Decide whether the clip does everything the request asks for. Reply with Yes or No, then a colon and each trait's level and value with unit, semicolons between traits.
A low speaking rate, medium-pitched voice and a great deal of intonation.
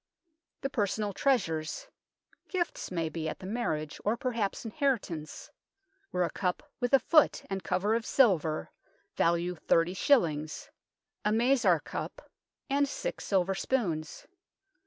No: slow, 130 wpm; high, 195 Hz; wide, 6.8 semitones